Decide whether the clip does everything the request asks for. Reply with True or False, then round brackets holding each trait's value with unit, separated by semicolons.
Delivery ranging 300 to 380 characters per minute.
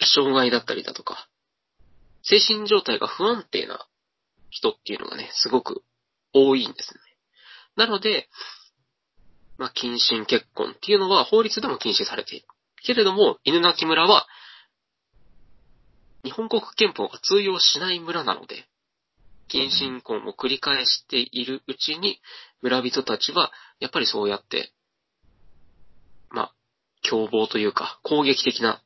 False (260 characters per minute)